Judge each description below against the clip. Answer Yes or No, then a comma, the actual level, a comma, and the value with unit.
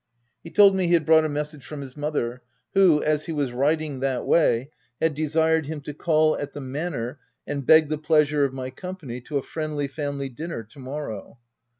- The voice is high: No, medium, 150 Hz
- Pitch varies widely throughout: No, average, 2.7 semitones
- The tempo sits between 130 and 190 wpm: No, fast, 205 wpm